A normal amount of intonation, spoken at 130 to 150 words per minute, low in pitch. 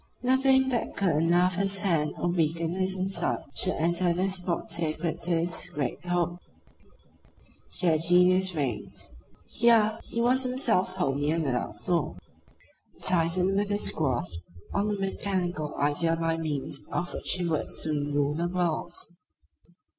No: average, 3.1 semitones; average, 145 wpm; medium, 175 Hz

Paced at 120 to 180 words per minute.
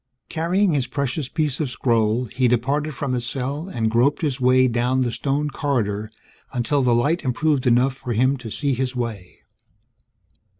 Yes: average, 170 wpm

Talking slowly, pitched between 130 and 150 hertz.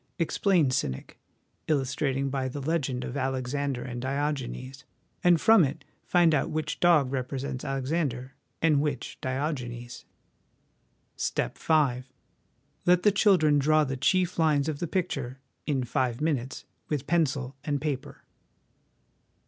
Yes: slow, 130 wpm; medium, 140 Hz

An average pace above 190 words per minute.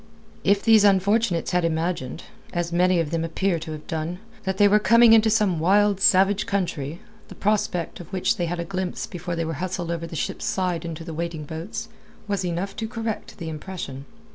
Yes: average, 200 wpm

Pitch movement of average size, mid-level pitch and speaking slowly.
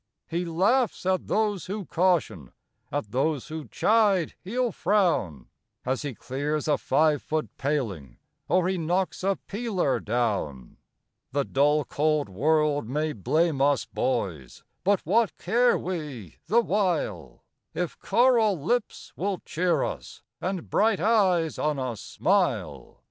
No: wide, 6.3 semitones; medium, 160 Hz; slow, 130 wpm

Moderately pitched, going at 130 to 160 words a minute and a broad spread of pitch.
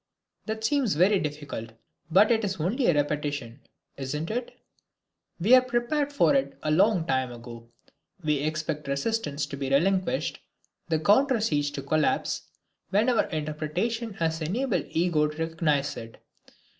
Yes: medium, 160 Hz; average, 150 wpm; wide, 7.1 semitones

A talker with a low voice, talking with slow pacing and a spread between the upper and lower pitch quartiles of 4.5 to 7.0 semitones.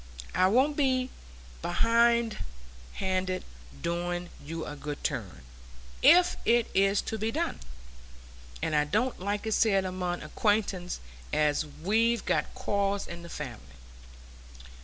No: high, 195 Hz; slow, 125 wpm; average, 5.1 semitones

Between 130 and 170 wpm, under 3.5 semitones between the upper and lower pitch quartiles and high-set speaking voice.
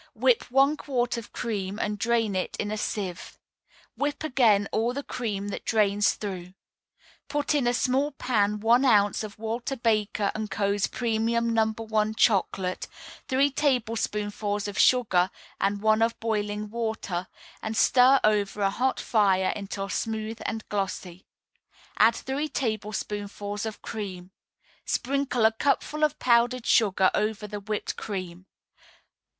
Yes: average, 140 wpm; average, 2.9 semitones; high, 220 Hz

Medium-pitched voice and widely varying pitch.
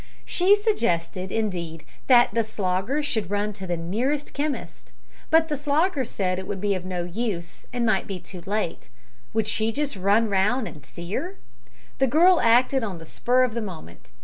No: high, 215 Hz; wide, 6.3 semitones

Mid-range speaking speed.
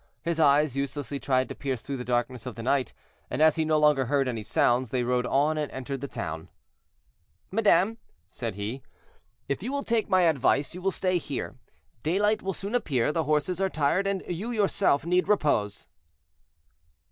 Yes: average, 185 wpm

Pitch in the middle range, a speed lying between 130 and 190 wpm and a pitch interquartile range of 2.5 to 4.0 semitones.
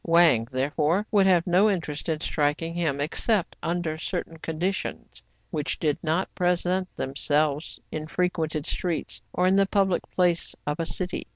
Yes: medium, 165 Hz; average, 155 wpm; average, 2.9 semitones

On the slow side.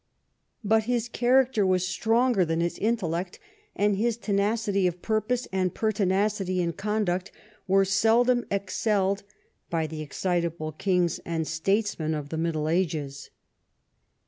Yes: slow, 125 wpm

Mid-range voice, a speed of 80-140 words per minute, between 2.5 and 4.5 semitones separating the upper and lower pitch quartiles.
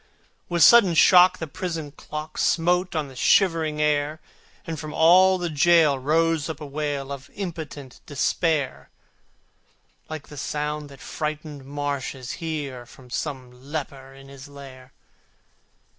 Yes: medium, 150 Hz; slow, 135 wpm; average, 2.8 semitones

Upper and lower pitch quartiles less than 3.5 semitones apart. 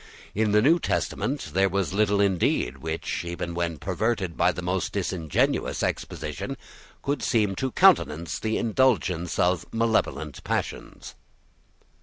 No: average, 4.5 semitones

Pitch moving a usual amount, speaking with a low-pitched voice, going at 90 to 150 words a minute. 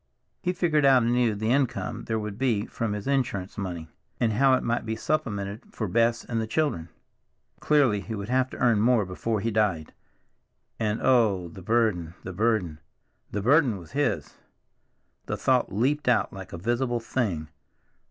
No: average, 3.8 semitones; low, 110 Hz; average, 170 wpm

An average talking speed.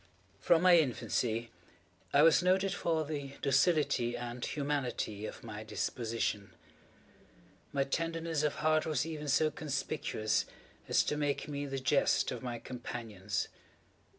No: slow, 130 wpm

